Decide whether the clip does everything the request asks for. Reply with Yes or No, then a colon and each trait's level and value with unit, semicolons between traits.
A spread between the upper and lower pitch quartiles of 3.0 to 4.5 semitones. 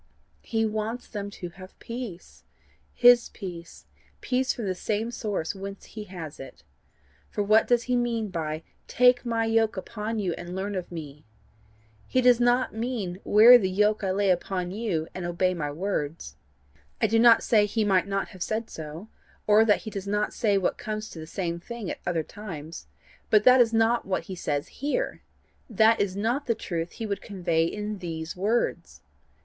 Yes: average, 4.1 semitones